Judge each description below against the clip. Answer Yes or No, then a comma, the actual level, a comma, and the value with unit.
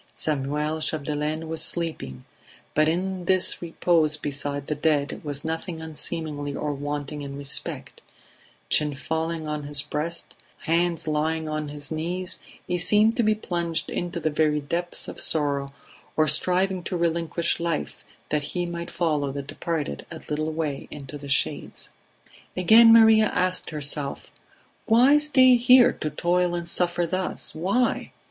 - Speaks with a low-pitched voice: No, medium, 160 Hz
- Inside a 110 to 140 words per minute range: No, average, 150 wpm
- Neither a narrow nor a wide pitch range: Yes, average, 3.0 semitones